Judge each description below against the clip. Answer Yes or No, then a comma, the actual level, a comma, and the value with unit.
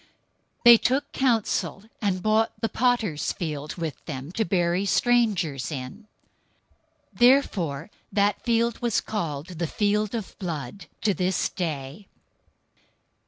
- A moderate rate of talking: No, slow, 125 wpm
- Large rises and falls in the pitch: Yes, wide, 5.7 semitones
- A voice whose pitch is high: Yes, high, 195 Hz